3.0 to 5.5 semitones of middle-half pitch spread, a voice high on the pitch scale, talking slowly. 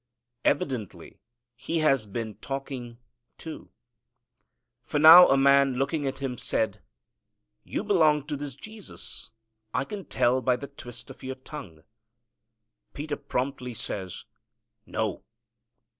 No: average, 3.3 semitones; low, 135 Hz; slow, 120 wpm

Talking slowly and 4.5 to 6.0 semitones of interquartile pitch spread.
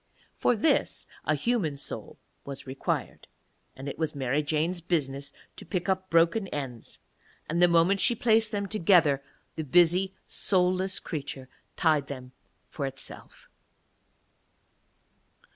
Yes: slow, 125 wpm; average, 5.1 semitones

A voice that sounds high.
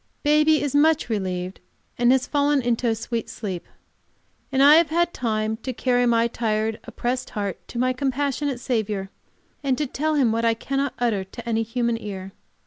Yes: high, 240 Hz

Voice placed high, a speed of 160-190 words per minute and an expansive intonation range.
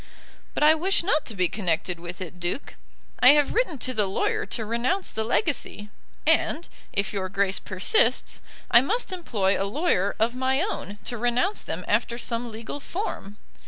Yes: high, 235 Hz; average, 175 wpm; wide, 7.5 semitones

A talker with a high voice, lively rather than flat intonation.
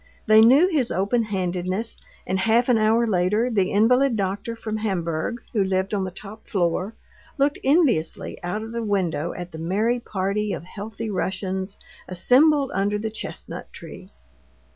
No: high, 210 Hz; average, 3.6 semitones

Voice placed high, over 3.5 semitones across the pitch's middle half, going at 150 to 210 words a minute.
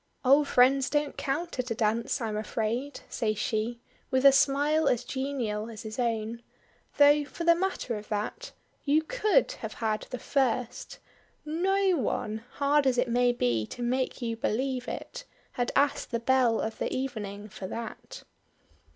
Yes: very high, 250 Hz; average, 4.3 semitones; average, 165 wpm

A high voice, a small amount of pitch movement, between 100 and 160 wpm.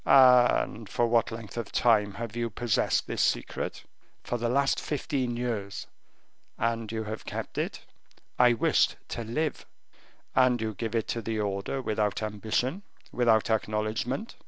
No: low, 115 Hz; narrow, 2.2 semitones; average, 150 wpm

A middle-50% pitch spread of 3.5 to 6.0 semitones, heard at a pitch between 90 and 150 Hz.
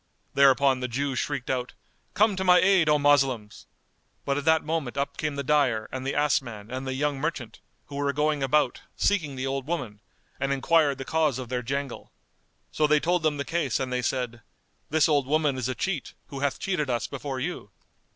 No: average, 2.8 semitones; medium, 140 Hz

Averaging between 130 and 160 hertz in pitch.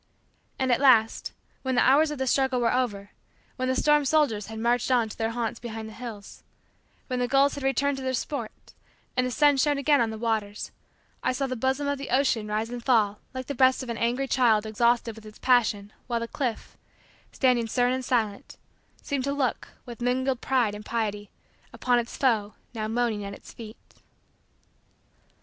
No: high, 245 Hz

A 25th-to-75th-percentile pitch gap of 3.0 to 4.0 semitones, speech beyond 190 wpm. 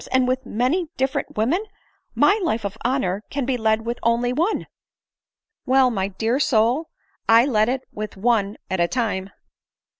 No: average, 3.6 semitones; average, 175 wpm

